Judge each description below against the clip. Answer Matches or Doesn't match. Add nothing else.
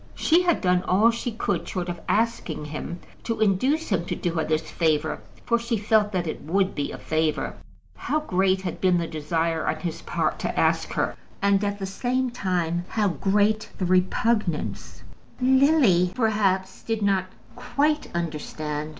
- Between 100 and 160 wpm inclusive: Doesn't match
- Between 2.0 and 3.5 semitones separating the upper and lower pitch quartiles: Doesn't match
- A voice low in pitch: Doesn't match